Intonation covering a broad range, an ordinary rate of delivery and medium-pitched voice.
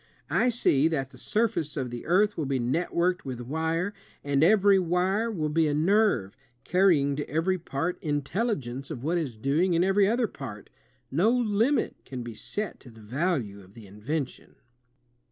Yes: wide, 6.2 semitones; average, 170 wpm; medium, 160 Hz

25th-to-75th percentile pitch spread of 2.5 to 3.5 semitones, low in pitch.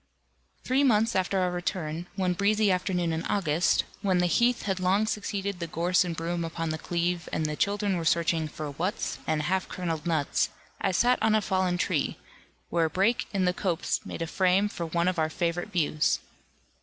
No: average, 3.0 semitones; medium, 180 Hz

